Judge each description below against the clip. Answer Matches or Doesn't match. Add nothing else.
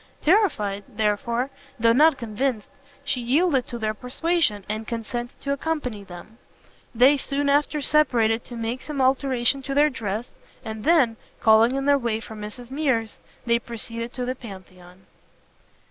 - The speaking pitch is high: Matches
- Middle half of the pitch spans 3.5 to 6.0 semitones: Matches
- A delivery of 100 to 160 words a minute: Matches